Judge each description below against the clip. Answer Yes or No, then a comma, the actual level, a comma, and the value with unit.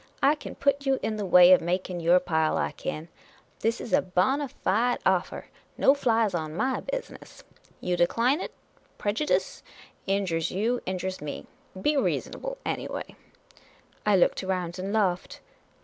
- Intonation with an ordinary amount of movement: No, wide, 5.8 semitones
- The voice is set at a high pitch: Yes, high, 195 Hz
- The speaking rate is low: No, average, 160 wpm